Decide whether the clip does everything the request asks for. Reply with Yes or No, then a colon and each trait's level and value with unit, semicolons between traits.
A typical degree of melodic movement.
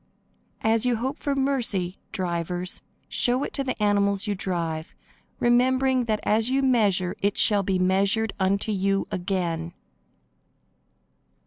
Yes: average, 4.7 semitones